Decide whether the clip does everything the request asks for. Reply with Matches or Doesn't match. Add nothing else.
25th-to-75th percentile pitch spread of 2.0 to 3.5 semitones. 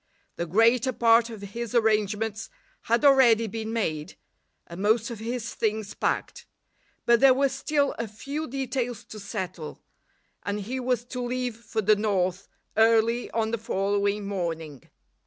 Matches